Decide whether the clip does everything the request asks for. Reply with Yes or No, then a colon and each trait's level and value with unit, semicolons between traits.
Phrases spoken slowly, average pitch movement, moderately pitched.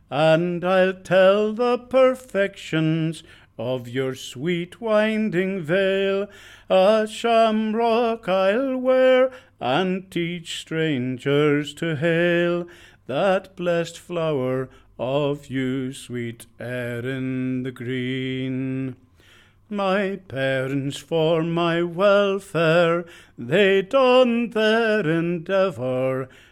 No: slow, 85 wpm; wide, 6.9 semitones; medium, 170 Hz